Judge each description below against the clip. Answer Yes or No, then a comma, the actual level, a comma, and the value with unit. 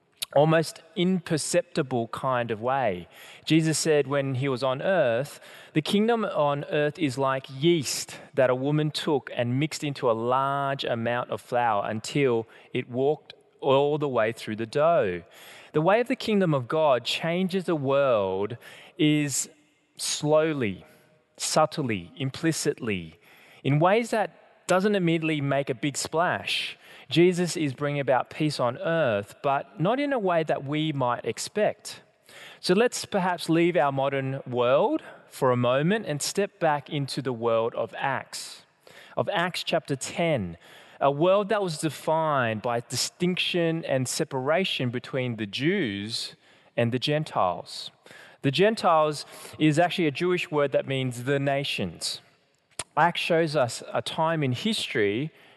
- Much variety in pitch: No, average, 4.4 semitones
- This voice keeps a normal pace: Yes, average, 145 wpm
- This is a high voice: No, medium, 145 Hz